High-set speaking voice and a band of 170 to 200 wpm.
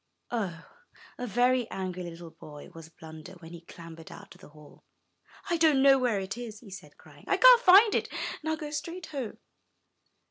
Yes: high, 215 Hz; average, 190 wpm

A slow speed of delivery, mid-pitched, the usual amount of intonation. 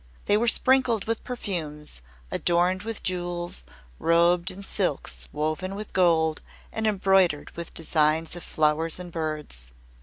Yes: slow, 130 wpm; medium, 175 Hz; average, 3.7 semitones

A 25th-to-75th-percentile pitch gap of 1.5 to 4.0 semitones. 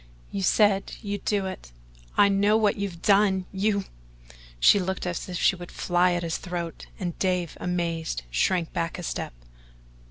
Yes: average, 2.8 semitones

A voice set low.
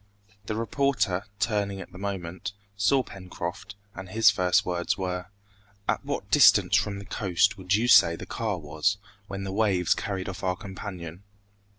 Yes: very low, 95 Hz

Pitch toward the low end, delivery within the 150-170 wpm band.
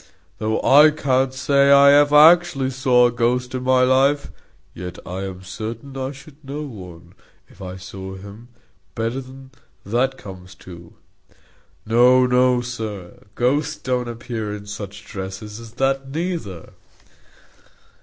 No: low, 125 Hz; average, 140 wpm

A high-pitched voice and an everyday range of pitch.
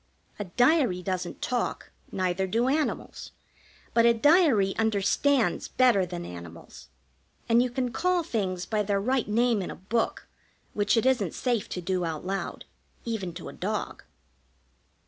Yes: high, 215 Hz; average, 4.9 semitones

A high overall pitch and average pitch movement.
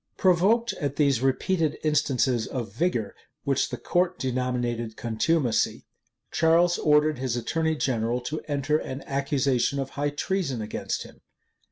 No: medium, 140 Hz; average, 4.3 semitones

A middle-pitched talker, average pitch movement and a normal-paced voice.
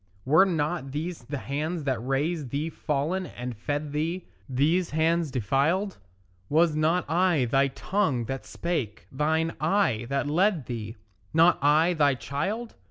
Yes: medium, 150 Hz; average, 4.0 semitones; average, 145 wpm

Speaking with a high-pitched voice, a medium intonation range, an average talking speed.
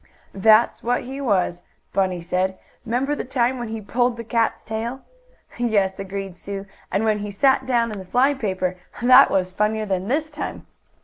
Yes: high, 220 Hz; average, 4.1 semitones; average, 180 wpm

